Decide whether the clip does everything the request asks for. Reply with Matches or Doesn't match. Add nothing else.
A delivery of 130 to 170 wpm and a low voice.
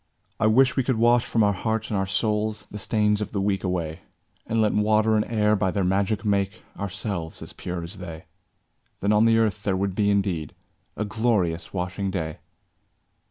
Doesn't match